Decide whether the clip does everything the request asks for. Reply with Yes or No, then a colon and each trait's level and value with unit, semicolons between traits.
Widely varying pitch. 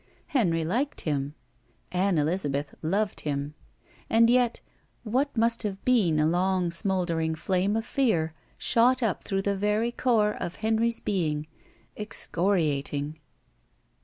Yes: wide, 5.8 semitones